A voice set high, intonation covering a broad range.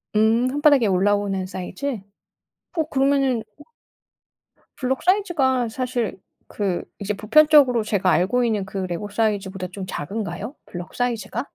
No: high, 220 Hz; average, 5.0 semitones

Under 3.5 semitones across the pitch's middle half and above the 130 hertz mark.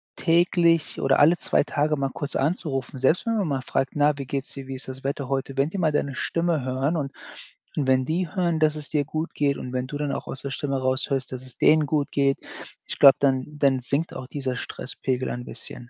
Yes: average, 2.7 semitones; medium, 140 Hz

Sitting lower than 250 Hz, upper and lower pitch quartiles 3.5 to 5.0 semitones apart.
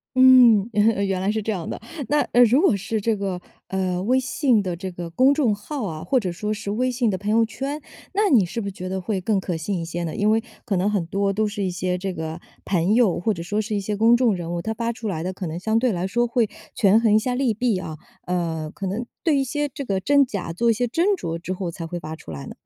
Yes: high, 205 Hz; average, 4.6 semitones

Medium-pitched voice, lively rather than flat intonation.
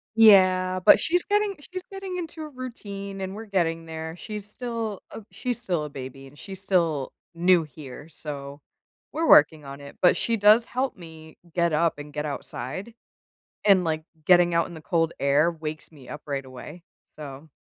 Yes: medium, 170 Hz; wide, 5.7 semitones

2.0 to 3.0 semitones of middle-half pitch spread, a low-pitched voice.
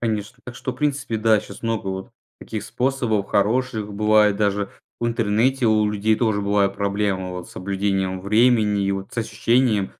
Yes: narrow, 2.6 semitones; low, 105 Hz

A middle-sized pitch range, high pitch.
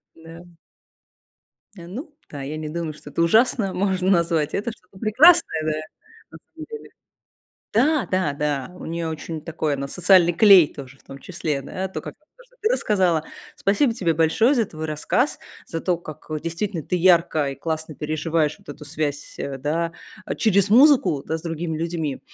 No: average, 4.3 semitones; medium, 170 Hz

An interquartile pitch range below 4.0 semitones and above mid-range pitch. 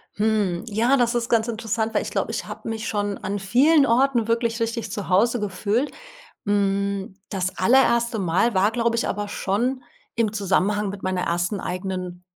Yes: average, 3.2 semitones; high, 210 Hz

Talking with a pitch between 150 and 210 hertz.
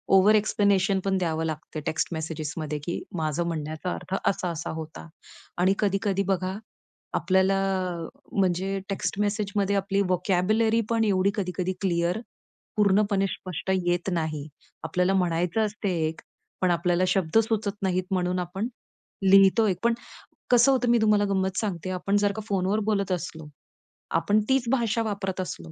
Yes: high, 190 Hz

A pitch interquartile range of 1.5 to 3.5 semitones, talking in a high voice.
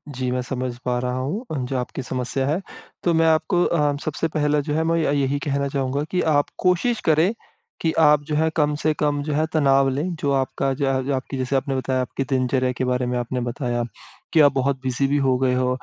No: average, 2.8 semitones; medium, 140 Hz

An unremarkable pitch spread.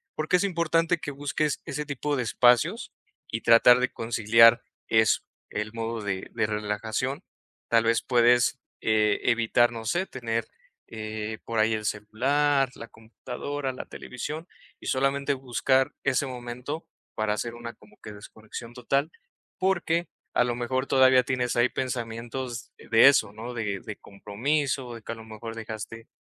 Yes: average, 3.5 semitones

